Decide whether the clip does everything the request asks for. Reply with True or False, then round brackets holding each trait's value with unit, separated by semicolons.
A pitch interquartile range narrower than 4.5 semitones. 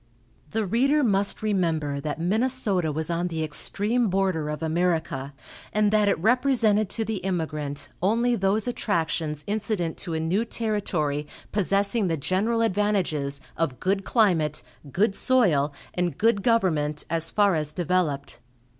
False (5.2 semitones)